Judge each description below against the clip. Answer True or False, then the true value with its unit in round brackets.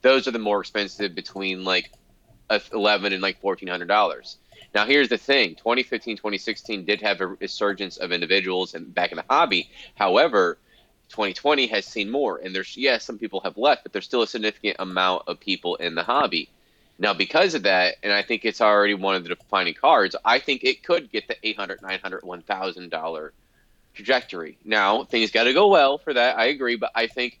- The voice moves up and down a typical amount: True (3.0 semitones)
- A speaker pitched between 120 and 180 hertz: False (100 Hz)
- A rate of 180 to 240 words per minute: True (195 wpm)